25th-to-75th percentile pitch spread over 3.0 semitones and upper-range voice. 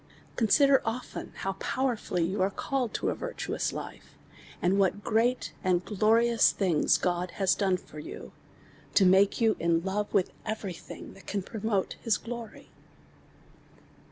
Yes: average, 3.6 semitones; high, 205 Hz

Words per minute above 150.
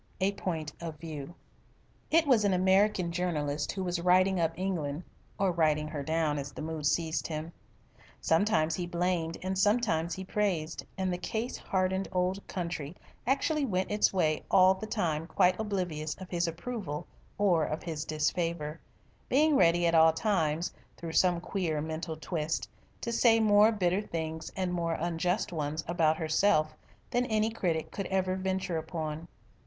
Yes: average, 160 wpm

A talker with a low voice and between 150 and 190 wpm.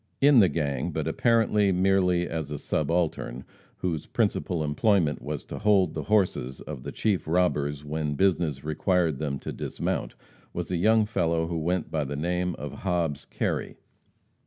Yes: very low, 85 Hz; average, 160 wpm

